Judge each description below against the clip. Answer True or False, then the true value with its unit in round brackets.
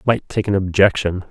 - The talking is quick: False (185 wpm)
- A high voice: False (95 Hz)